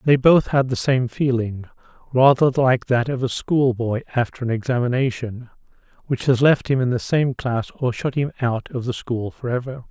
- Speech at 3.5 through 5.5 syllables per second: Yes, 4.9 syllables/s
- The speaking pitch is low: Yes, low, 125 Hz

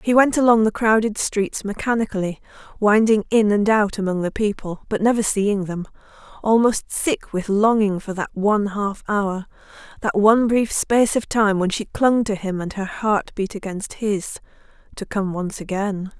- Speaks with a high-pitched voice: Yes, high, 205 Hz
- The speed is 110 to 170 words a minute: Yes, average, 165 wpm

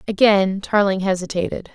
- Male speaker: No, female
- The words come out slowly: Yes, slow, 105 wpm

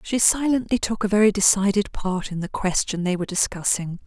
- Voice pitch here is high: Yes, high, 200 Hz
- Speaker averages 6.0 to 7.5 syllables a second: No, 5.6 syllables/s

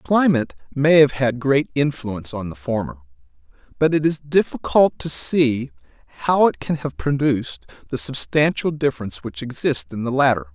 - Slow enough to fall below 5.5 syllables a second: Yes, 5.1 syllables/s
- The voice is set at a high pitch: No, low, 130 Hz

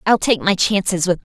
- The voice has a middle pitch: No, high, 195 Hz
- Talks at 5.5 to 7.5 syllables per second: Yes, 5.6 syllables/s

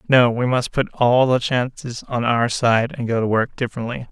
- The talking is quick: Yes, fast, 220 wpm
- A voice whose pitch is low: Yes, low, 120 Hz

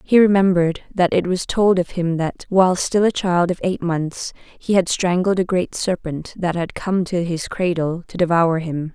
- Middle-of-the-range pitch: Yes, medium, 175 Hz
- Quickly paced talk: Yes, fast, 210 wpm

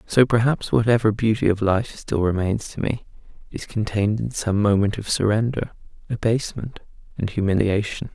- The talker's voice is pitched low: Yes, low, 110 Hz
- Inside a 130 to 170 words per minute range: Yes, average, 145 wpm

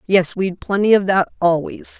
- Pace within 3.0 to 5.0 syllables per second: Yes, 4.6 syllables/s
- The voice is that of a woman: Yes, female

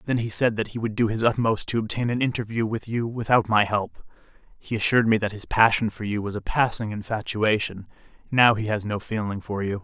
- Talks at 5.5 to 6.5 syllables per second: Yes, 5.7 syllables/s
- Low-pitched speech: Yes, low, 110 Hz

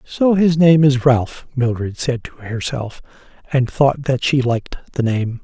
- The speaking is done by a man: Yes, male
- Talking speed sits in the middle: Yes, average, 175 wpm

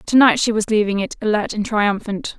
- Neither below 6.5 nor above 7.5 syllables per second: No, 5.4 syllables/s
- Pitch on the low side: No, high, 215 Hz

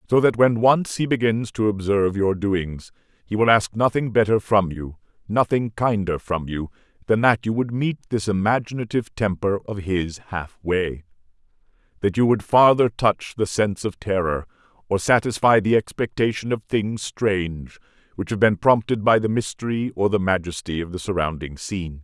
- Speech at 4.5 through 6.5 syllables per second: Yes, 5.0 syllables/s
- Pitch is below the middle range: Yes, low, 105 Hz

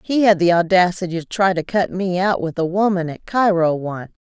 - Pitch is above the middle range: No, medium, 180 Hz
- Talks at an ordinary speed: No, fast, 225 wpm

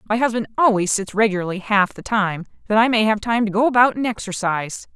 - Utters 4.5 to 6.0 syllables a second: No, 6.2 syllables/s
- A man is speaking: No, female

